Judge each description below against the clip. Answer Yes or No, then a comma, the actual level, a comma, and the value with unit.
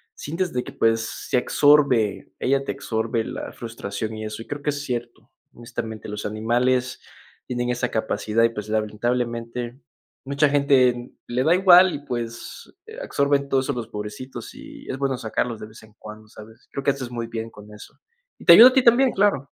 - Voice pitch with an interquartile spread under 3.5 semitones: No, average, 3.8 semitones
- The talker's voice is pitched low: Yes, low, 120 Hz